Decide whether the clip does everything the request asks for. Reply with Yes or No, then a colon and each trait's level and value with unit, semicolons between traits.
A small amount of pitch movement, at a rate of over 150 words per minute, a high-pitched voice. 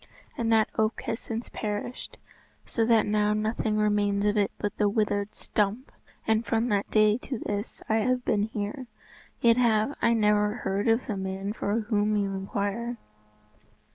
Yes: narrow, 1.7 semitones; average, 170 wpm; high, 215 Hz